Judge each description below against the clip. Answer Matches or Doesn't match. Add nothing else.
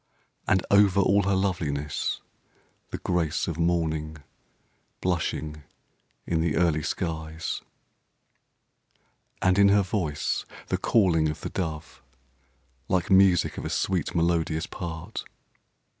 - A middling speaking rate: Doesn't match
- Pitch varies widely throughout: Doesn't match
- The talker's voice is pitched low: Matches